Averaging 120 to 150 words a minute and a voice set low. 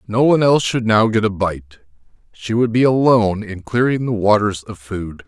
No: fast, 205 wpm; low, 110 Hz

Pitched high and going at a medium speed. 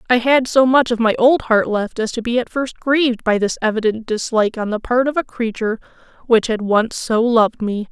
No: high, 235 Hz; fast, 235 wpm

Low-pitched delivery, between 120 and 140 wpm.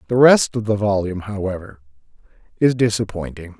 Yes: low, 100 Hz; slow, 135 wpm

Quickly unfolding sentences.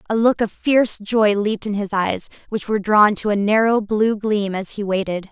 Yes: fast, 225 wpm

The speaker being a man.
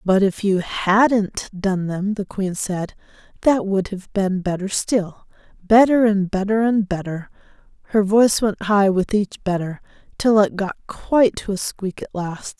No: female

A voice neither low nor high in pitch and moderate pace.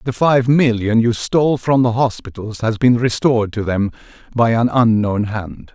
No: low, 115 Hz; average, 175 wpm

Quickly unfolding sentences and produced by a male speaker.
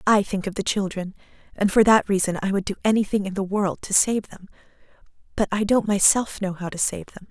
No: fast, 230 wpm; female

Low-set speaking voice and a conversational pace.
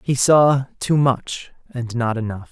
Yes: low, 130 Hz; average, 165 wpm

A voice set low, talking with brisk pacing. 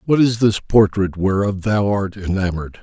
No: low, 100 Hz; average, 170 wpm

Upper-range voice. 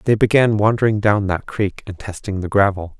No: low, 105 Hz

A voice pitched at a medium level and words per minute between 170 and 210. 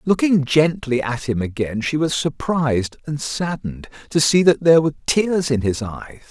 Yes: medium, 145 Hz; average, 180 wpm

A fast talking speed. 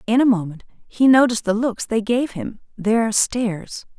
No: average, 165 wpm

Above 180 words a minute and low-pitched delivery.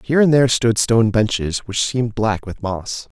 Yes: fast, 205 wpm; low, 115 Hz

